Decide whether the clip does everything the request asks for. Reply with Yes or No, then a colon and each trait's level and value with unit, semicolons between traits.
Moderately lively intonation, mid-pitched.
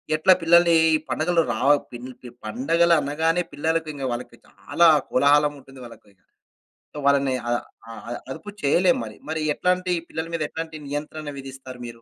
Yes: average, 3.7 semitones; medium, 150 Hz